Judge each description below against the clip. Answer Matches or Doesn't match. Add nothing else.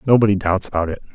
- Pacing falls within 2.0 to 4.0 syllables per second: Doesn't match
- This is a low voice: Matches